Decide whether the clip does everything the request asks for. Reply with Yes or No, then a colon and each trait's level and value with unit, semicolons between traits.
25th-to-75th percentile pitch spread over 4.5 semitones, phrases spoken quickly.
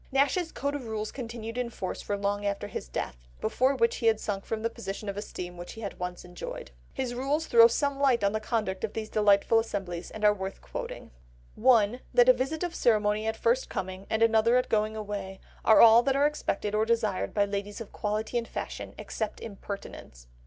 No: average, 3.1 semitones; fast, 210 wpm